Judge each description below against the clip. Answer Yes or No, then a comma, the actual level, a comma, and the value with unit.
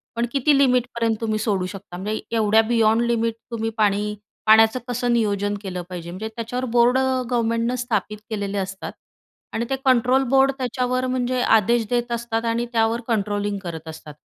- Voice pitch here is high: Yes, high, 230 Hz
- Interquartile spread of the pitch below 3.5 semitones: Yes, average, 3.0 semitones